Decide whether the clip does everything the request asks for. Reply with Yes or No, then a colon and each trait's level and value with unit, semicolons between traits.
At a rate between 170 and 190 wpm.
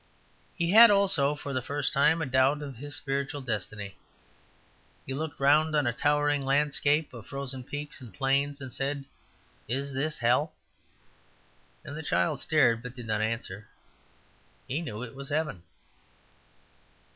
No: average, 155 wpm